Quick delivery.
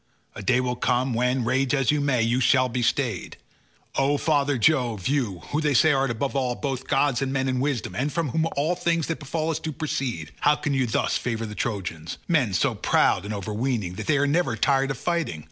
Yes: fast, 220 wpm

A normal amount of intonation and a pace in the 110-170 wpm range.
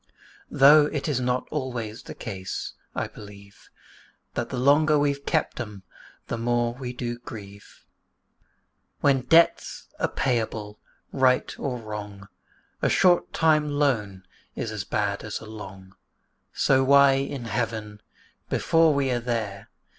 Yes: average, 4.7 semitones; average, 140 wpm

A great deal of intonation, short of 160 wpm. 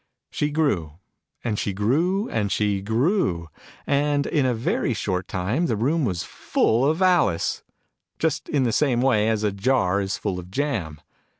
No: wide, 6.8 semitones; average, 170 wpm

